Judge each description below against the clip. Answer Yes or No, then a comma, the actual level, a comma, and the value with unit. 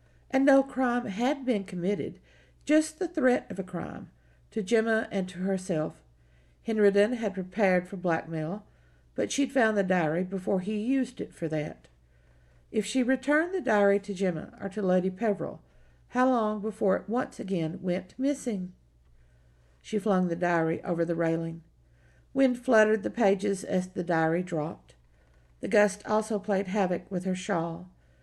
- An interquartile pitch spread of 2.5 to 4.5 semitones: No, average, 5.1 semitones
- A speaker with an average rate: Yes, average, 160 wpm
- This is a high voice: Yes, high, 195 Hz